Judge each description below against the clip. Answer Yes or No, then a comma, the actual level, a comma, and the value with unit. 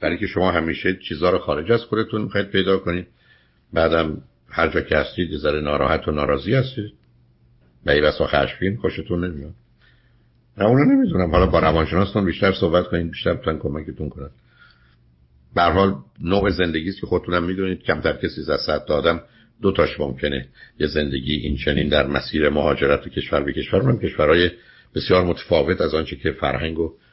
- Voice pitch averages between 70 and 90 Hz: Yes, very low, 85 Hz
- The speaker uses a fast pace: Yes, fast, 170 wpm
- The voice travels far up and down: No, average, 4.8 semitones